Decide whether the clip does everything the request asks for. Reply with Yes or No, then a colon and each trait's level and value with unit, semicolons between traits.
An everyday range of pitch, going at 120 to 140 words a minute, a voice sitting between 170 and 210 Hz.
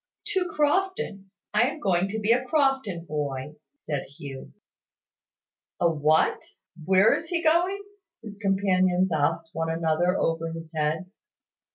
No: wide, 7.9 semitones; slow, 135 wpm; medium, 185 Hz